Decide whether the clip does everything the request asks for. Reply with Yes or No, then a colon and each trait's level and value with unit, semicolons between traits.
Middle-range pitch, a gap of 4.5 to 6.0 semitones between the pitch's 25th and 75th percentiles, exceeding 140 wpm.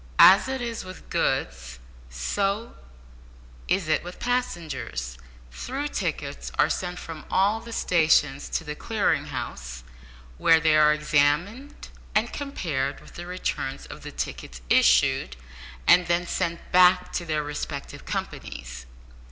No: medium, 165 Hz; wide, 5.5 semitones; slow, 135 wpm